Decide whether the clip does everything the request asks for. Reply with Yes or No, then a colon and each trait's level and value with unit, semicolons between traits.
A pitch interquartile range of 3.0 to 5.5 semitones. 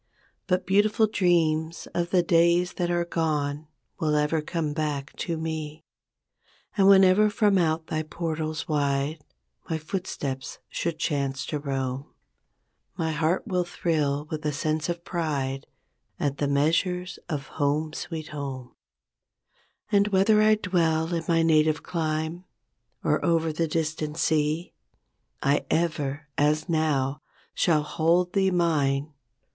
No: narrow, 2.5 semitones